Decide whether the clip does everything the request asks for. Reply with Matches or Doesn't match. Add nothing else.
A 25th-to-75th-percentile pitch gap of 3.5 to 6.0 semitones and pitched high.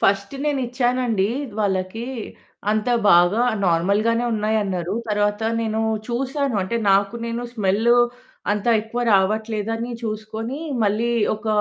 Doesn't match